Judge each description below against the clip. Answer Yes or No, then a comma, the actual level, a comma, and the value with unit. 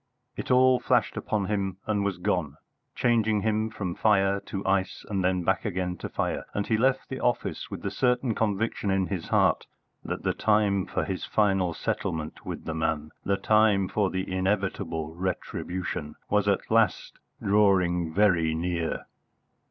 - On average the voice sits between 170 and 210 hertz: No, low, 100 Hz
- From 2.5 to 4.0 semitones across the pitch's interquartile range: Yes, average, 2.9 semitones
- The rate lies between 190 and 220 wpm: No, average, 165 wpm